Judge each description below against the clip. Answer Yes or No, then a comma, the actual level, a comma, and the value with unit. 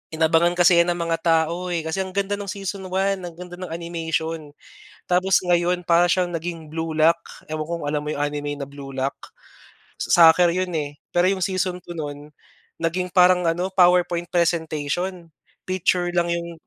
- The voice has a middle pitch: Yes, medium, 170 Hz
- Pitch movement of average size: No, narrow, 1.9 semitones